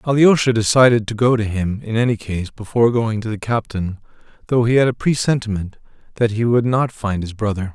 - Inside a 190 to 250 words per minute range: Yes, average, 200 wpm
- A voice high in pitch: No, low, 115 Hz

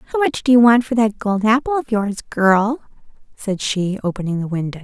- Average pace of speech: No, fast, 210 wpm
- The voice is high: Yes, high, 215 Hz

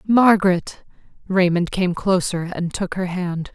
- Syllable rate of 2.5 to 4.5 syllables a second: Yes, 4.0 syllables/s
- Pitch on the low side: No, medium, 185 Hz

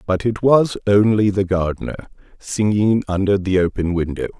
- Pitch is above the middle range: No, low, 100 Hz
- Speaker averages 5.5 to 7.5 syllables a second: No, 5.1 syllables/s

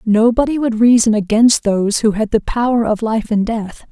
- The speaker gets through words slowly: No, average, 200 wpm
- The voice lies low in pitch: No, high, 225 Hz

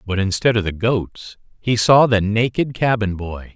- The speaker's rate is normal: Yes, average, 185 wpm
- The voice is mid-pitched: No, low, 110 Hz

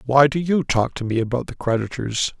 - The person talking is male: Yes, male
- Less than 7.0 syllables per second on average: Yes, 5.4 syllables/s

